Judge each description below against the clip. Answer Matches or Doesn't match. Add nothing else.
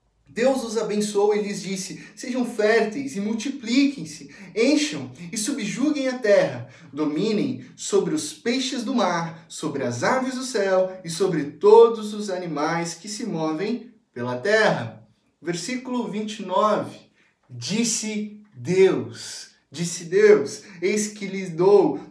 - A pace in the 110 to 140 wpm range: Matches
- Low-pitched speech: Doesn't match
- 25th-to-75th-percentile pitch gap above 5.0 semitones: Matches